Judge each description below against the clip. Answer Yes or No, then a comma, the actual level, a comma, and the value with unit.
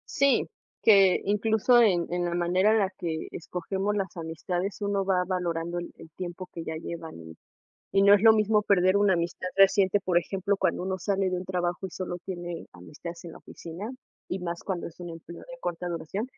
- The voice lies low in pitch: No, medium, 180 Hz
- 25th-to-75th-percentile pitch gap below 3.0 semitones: Yes, narrow, 2.5 semitones